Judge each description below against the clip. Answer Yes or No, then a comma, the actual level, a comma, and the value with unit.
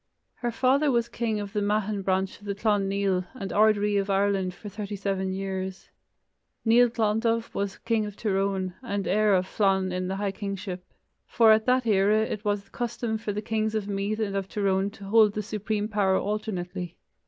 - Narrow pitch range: Yes, narrow, 2.0 semitones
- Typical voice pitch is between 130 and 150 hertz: No, high, 205 Hz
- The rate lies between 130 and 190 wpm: No, average, 200 wpm